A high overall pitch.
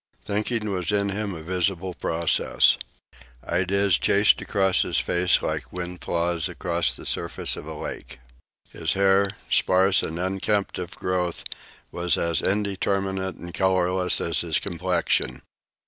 No: very low, 95 Hz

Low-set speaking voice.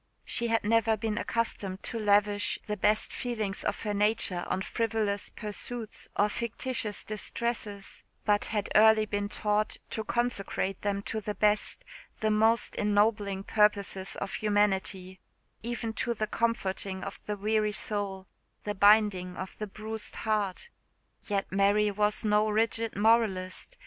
No: high, 210 Hz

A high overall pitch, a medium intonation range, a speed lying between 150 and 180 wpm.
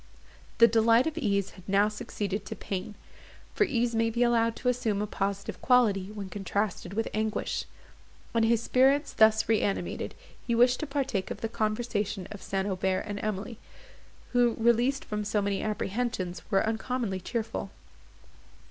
Yes: high, 220 Hz; average, 3.0 semitones; average, 155 wpm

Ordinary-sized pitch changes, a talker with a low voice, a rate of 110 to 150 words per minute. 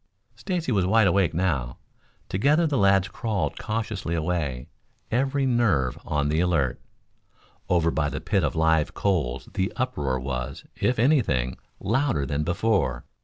No: wide, 7.8 semitones; very low, 90 Hz; average, 145 wpm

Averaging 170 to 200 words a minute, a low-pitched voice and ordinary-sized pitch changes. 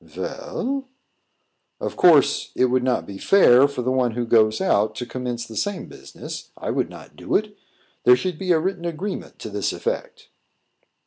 No: average, 180 wpm; low, 130 Hz; wide, 7.3 semitones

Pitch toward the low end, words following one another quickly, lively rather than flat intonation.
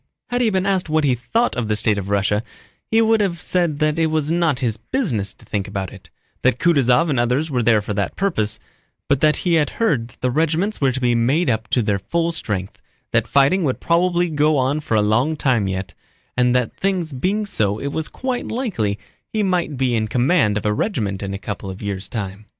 Yes: low, 130 Hz; fast, 230 wpm; wide, 7.9 semitones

